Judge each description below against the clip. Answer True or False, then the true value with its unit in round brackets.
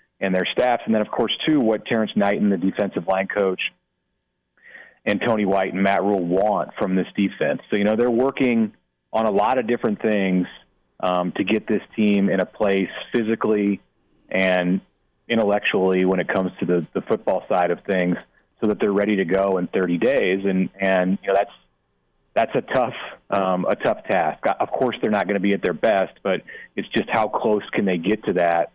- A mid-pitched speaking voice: False (95 Hz)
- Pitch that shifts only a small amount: True (2.2 semitones)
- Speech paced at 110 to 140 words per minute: False (205 wpm)